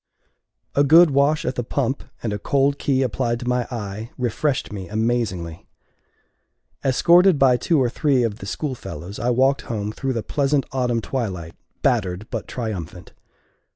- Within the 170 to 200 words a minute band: No, average, 155 wpm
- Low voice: Yes, low, 120 Hz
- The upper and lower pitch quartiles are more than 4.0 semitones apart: Yes, average, 4.4 semitones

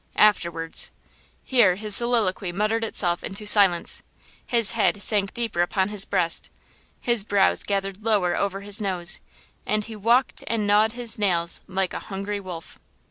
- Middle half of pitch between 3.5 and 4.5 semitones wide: No, narrow, 2.5 semitones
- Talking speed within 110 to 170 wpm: Yes, average, 150 wpm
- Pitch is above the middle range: Yes, high, 205 Hz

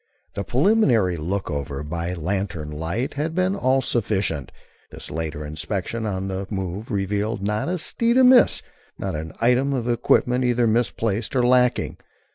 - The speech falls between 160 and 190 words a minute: No, average, 150 wpm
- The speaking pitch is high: No, low, 105 Hz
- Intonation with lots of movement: Yes, wide, 6.1 semitones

